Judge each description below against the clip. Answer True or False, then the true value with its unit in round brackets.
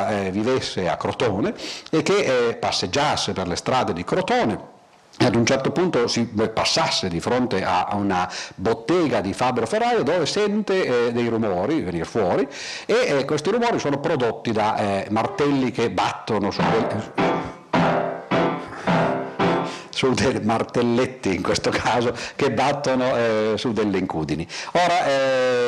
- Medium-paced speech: True (145 wpm)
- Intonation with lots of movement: False (4.1 semitones)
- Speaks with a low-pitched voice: True (120 Hz)